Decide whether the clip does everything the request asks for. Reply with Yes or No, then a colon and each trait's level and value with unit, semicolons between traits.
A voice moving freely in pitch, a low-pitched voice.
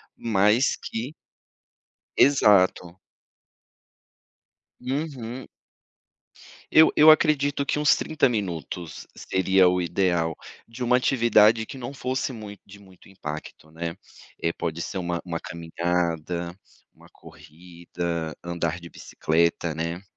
Yes: wide, 6.2 semitones; very low, 95 Hz